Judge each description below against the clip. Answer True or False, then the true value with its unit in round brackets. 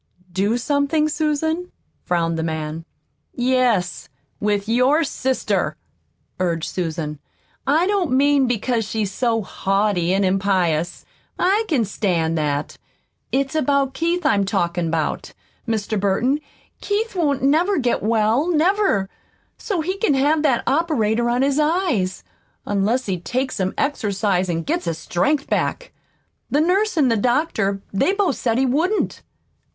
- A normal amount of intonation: False (7.8 semitones)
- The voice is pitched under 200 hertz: False (245 Hz)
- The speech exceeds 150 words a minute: False (135 wpm)